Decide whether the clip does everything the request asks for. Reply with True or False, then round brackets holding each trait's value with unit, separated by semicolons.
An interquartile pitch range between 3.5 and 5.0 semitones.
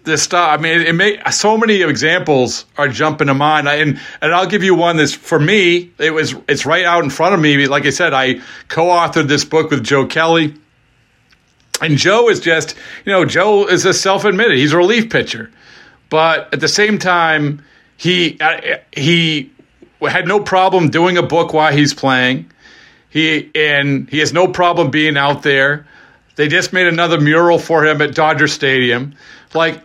False (3.1 semitones)